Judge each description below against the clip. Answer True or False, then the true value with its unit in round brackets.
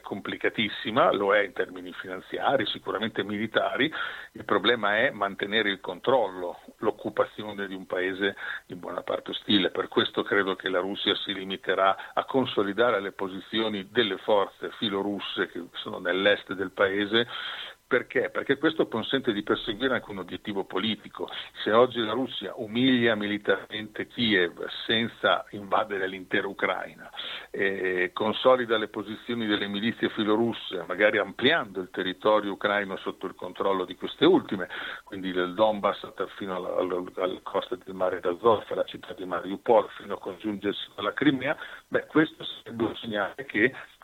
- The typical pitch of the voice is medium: False (105 Hz)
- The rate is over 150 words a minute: False (145 wpm)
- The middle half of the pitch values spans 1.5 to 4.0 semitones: True (2.5 semitones)